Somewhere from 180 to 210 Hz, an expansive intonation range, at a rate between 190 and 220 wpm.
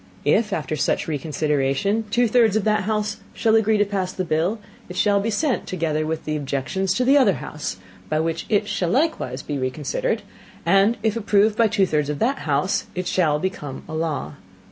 Yes: high, 190 Hz; wide, 6.0 semitones; average, 195 wpm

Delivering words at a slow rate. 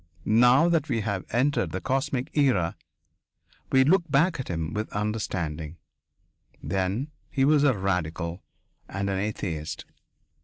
Yes: slow, 130 wpm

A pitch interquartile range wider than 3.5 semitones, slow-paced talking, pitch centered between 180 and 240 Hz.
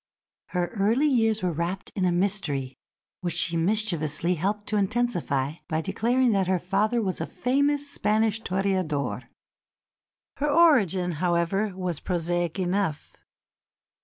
Yes: average, 4.1 semitones; slow, 130 wpm; high, 190 Hz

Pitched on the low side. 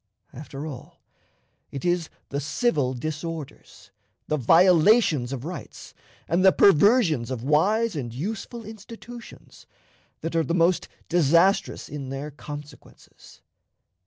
No: medium, 160 Hz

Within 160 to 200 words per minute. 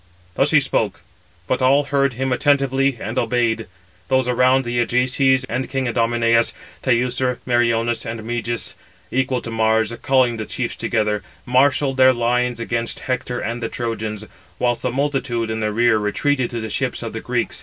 Yes: average, 165 wpm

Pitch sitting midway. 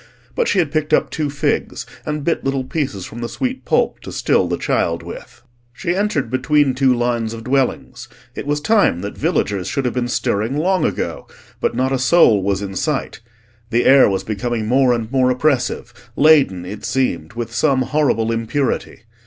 No: low, 130 Hz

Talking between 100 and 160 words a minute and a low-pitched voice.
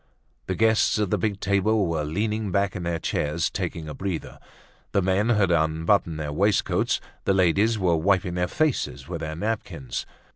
No: average, 175 wpm; very low, 95 Hz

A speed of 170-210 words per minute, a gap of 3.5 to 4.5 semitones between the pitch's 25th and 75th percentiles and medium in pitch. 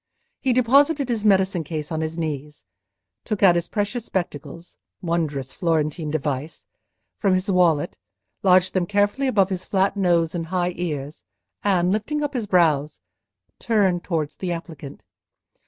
No: average, 145 wpm; average, 4.2 semitones; medium, 180 Hz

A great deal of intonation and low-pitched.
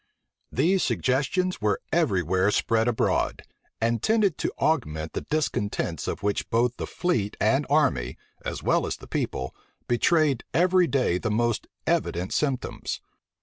Yes: wide, 7.3 semitones; low, 120 Hz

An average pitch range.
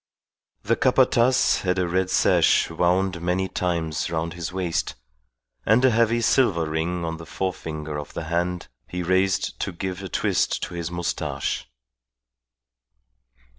No: narrow, 2.2 semitones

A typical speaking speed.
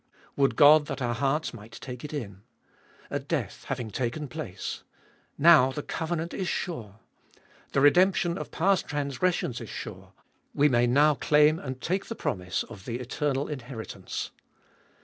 Yes: average, 150 wpm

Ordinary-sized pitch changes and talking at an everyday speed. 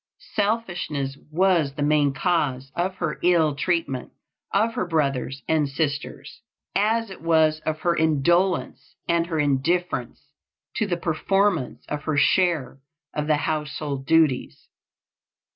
No: average, 3.6 semitones; slow, 125 wpm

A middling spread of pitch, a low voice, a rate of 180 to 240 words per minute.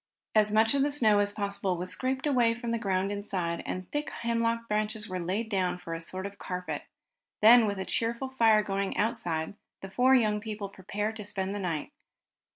No: average, 3.4 semitones; high, 210 Hz; average, 200 wpm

